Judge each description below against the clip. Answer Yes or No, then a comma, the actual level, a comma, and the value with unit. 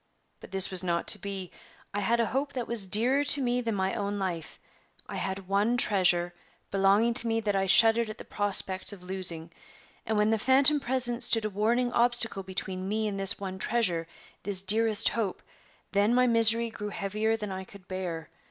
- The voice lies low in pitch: No, high, 205 Hz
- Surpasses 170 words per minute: Yes, average, 200 wpm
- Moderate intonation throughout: Yes, average, 3.5 semitones